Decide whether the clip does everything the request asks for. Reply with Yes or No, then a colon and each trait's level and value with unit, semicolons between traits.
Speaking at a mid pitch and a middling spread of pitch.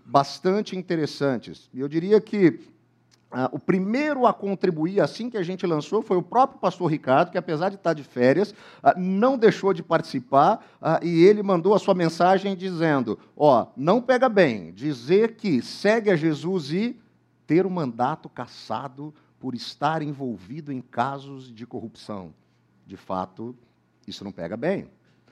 No: medium, 165 Hz; wide, 7.0 semitones